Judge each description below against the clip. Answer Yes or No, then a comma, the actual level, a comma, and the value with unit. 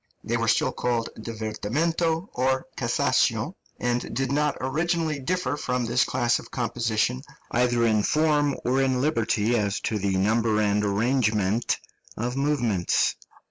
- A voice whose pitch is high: No, low, 120 Hz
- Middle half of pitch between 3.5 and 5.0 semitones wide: Yes, average, 4.1 semitones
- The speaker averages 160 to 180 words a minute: No, average, 140 wpm